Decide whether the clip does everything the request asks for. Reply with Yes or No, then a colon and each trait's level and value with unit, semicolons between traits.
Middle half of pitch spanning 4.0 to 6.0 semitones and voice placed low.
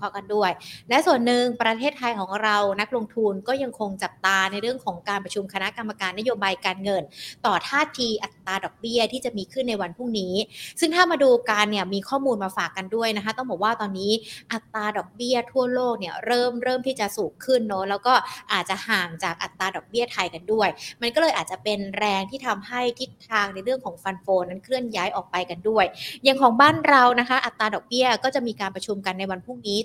No: average, 4.3 semitones; high, 215 Hz